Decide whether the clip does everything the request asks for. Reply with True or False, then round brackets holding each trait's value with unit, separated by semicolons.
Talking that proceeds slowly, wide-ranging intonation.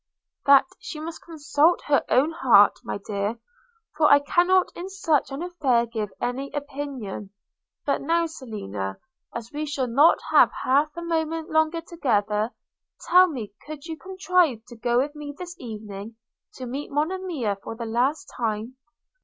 False (155 wpm; 5.9 semitones)